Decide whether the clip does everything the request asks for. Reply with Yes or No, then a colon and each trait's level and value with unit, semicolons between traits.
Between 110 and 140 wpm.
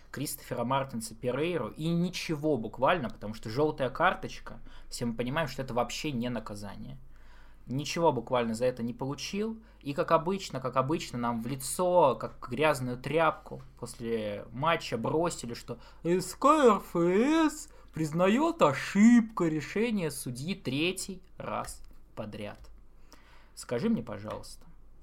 Yes: average, 120 wpm